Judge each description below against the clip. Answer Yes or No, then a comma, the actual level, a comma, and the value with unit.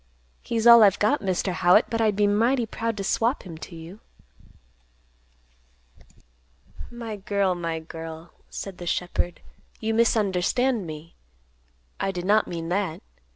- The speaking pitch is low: No, high, 200 Hz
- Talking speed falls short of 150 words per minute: Yes, average, 140 wpm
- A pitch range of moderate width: Yes, average, 4.2 semitones